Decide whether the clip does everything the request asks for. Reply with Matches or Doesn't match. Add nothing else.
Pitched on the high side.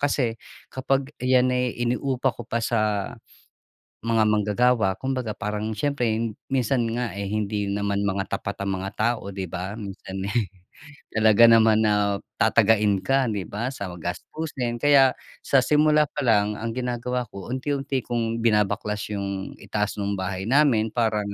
Doesn't match